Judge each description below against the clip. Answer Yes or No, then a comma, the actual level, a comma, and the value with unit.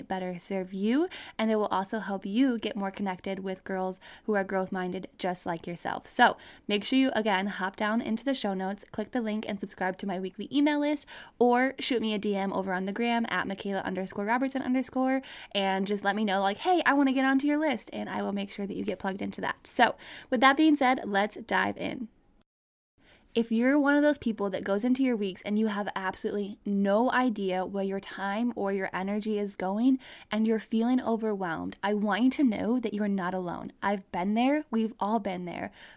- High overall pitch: Yes, high, 210 Hz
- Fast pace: Yes, fast, 220 wpm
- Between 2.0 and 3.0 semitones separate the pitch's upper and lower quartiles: No, average, 4.3 semitones